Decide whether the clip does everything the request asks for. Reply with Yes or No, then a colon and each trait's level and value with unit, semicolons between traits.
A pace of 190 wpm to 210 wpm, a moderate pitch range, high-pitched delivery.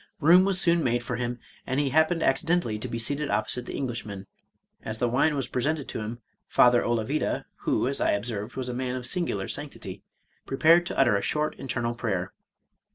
No: fast, 205 wpm; average, 4.5 semitones; low, 125 Hz